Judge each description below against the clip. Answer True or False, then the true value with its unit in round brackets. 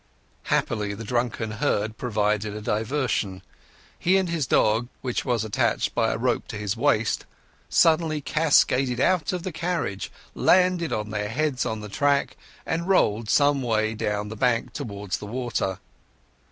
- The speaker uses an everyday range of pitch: False (5.9 semitones)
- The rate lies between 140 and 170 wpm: True (155 wpm)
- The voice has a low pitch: True (120 Hz)